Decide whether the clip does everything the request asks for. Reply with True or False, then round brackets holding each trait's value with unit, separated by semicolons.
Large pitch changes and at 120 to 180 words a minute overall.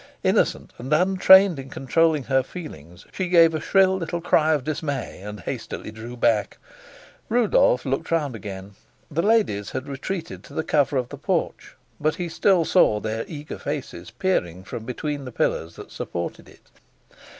True (6.9 semitones; 165 wpm)